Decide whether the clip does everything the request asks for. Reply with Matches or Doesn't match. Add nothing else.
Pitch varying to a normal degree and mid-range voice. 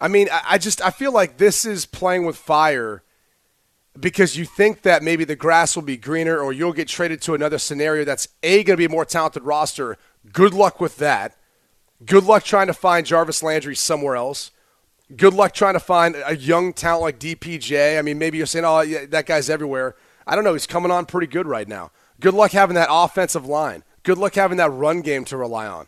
Matches